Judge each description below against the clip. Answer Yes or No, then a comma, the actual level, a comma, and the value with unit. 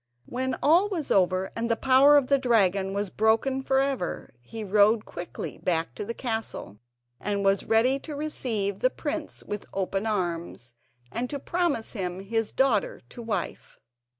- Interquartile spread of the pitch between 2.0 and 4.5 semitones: No, wide, 5.4 semitones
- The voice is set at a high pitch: Yes, high, 225 Hz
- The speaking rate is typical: Yes, average, 165 wpm